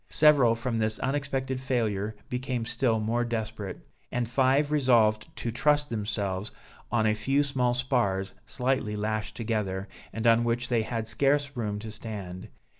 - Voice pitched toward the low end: Yes, low, 115 Hz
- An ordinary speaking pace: Yes, average, 150 wpm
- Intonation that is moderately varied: Yes, average, 3.4 semitones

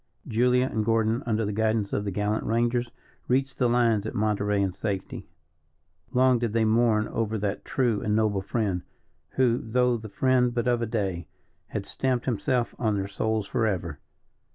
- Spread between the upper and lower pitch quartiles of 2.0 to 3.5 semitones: Yes, average, 2.8 semitones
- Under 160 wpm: No, average, 175 wpm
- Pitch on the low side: Yes, low, 110 Hz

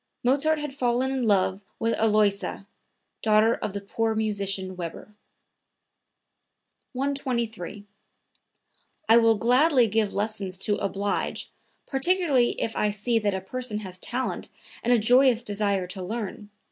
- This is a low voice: No, high, 220 Hz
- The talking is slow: Yes, slow, 130 wpm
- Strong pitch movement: No, average, 3.5 semitones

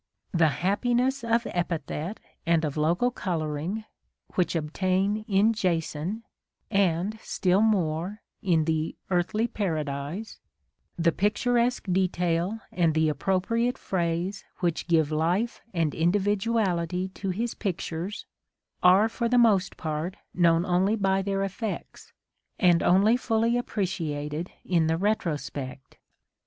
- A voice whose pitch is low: No, medium, 185 Hz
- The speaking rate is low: Yes, slow, 120 wpm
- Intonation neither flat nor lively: Yes, average, 4.3 semitones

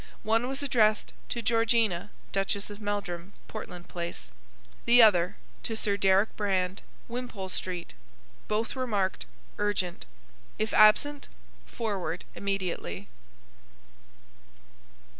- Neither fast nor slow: No, slow, 105 wpm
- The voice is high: Yes, high, 205 Hz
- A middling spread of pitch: Yes, average, 3.4 semitones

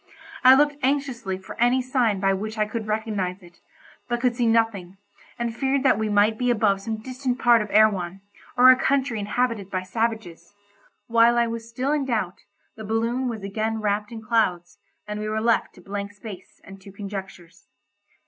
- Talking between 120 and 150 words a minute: No, average, 185 wpm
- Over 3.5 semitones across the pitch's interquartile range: No, average, 3.2 semitones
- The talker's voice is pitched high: Yes, high, 220 Hz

